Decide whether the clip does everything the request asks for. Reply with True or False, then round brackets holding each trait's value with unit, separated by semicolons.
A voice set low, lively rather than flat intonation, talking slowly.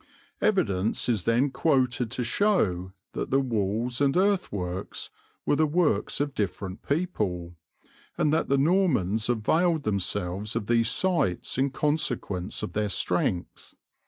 True (120 Hz; 7.1 semitones; 130 wpm)